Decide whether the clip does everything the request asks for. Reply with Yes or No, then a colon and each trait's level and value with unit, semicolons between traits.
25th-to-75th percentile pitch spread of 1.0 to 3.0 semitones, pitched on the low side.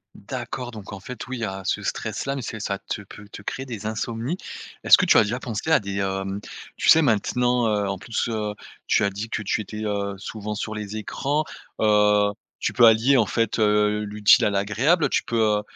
Yes: average, 2.7 semitones; low, 105 Hz